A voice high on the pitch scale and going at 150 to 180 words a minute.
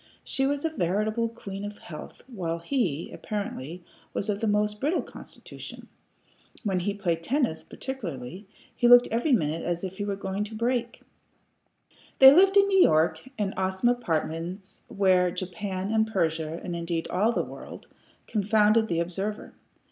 Yes: high, 200 Hz; average, 155 wpm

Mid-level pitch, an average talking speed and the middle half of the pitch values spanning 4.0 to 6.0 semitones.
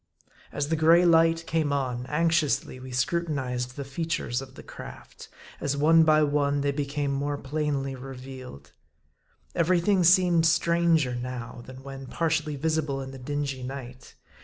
No: medium, 145 Hz; average, 150 wpm; average, 3.6 semitones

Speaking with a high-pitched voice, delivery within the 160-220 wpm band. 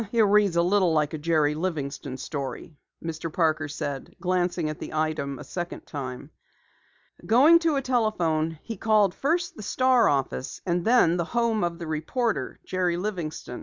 No: medium, 175 Hz; average, 165 wpm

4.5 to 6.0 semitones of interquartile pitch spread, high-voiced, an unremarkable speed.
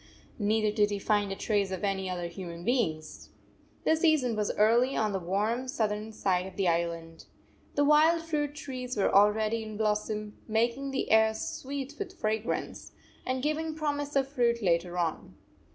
Yes: wide, 5.4 semitones; high, 220 Hz; average, 170 wpm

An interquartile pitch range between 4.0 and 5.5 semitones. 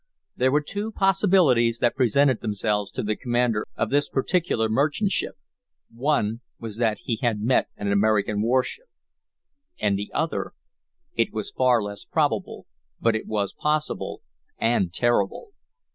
Yes: average, 5.0 semitones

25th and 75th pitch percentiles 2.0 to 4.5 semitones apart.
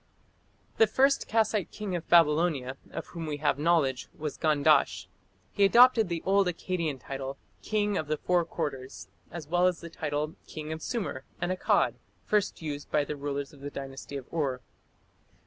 Yes: average, 4.1 semitones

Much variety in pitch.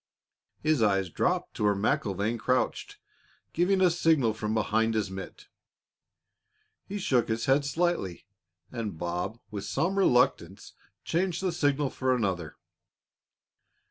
Yes: wide, 7.4 semitones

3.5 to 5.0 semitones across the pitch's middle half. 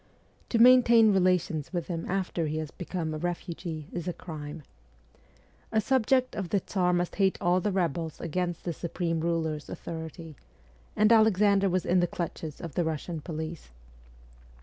No: average, 3.1 semitones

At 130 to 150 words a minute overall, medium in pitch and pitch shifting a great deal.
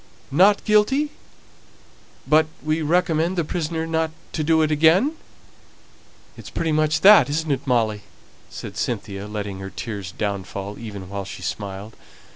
Yes: average, 140 wpm; medium, 150 Hz; wide, 8.1 semitones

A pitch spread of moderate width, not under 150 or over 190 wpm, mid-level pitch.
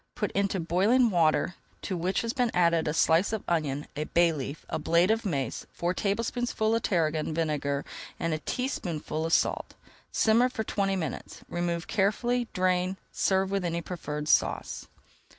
Yes: average, 4.4 semitones; average, 170 wpm; medium, 180 Hz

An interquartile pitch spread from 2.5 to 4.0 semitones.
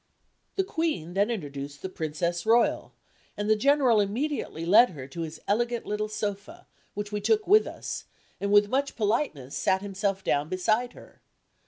No: wide, 5.4 semitones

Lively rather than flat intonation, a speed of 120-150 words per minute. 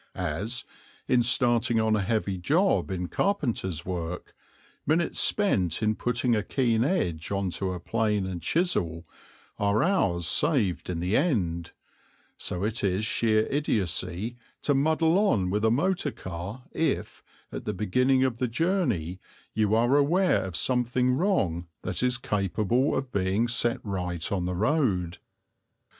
Yes: wide, 6.0 semitones; average, 145 wpm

